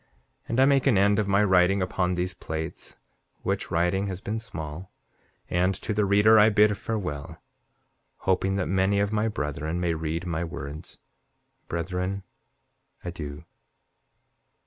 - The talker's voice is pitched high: No, very low, 95 Hz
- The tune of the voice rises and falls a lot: No, average, 3.3 semitones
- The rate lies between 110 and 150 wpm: Yes, average, 145 wpm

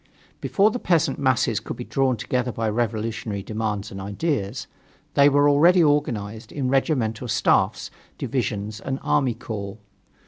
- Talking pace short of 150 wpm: Yes, average, 140 wpm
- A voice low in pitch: Yes, low, 120 Hz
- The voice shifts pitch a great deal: No, average, 4.9 semitones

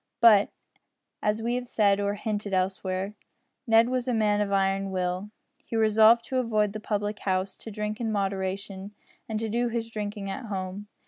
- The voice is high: Yes, high, 210 Hz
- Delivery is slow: No, average, 180 wpm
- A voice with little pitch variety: Yes, narrow, 2.3 semitones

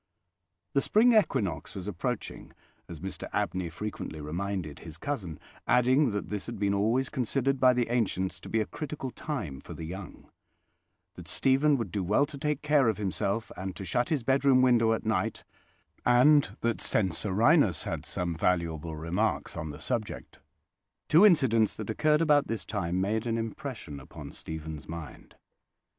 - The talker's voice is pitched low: Yes, low, 110 Hz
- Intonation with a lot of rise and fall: Yes, wide, 6.6 semitones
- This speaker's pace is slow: No, average, 165 wpm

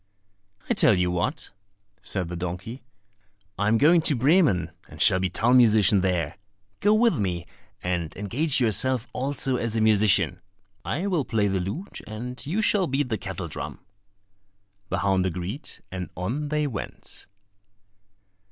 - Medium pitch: No, low, 110 Hz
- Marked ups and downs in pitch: Yes, wide, 6.9 semitones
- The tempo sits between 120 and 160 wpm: Yes, average, 150 wpm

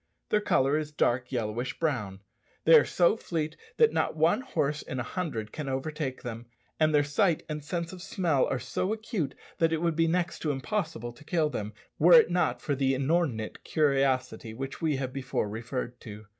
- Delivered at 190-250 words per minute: Yes, average, 195 wpm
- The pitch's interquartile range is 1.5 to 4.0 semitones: No, average, 4.5 semitones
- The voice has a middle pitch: Yes, medium, 145 Hz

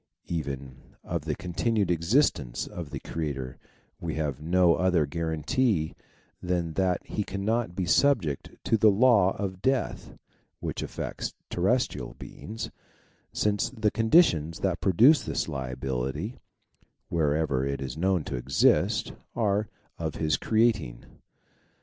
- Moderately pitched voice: No, very low, 85 Hz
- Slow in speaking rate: Yes, slow, 125 wpm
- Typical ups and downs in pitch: No, wide, 6.0 semitones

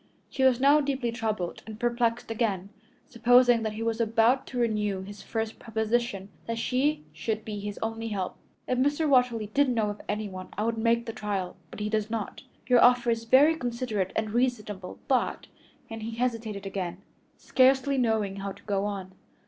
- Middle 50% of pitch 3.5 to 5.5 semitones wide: No, average, 2.9 semitones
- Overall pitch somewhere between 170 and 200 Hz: No, high, 225 Hz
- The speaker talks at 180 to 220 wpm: Yes, average, 185 wpm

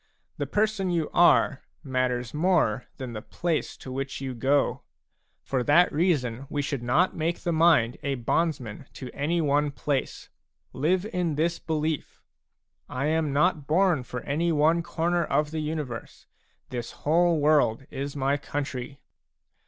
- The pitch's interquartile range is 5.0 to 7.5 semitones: No, average, 4.0 semitones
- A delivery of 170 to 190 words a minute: No, average, 155 wpm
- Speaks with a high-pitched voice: No, medium, 150 Hz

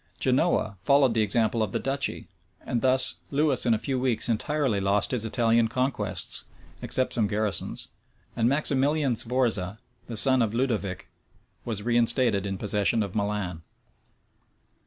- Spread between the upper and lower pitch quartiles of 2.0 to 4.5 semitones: Yes, average, 3.8 semitones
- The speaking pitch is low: Yes, low, 115 Hz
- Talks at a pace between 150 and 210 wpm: No, average, 140 wpm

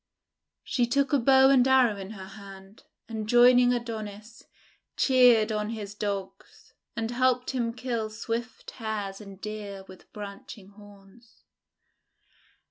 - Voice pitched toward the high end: Yes, high, 220 Hz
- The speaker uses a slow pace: Yes, slow, 125 wpm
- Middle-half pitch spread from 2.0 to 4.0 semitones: Yes, average, 3.2 semitones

